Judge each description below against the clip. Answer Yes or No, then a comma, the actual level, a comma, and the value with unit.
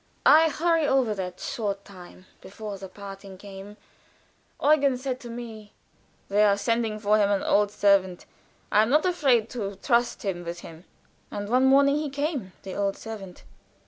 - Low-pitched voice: No, high, 210 Hz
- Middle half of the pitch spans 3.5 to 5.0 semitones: Yes, average, 4.6 semitones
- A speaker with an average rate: Yes, average, 170 wpm